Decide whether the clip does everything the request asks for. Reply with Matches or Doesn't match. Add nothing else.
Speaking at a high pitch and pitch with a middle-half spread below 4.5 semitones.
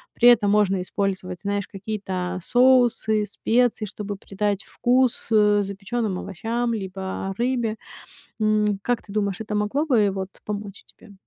Matches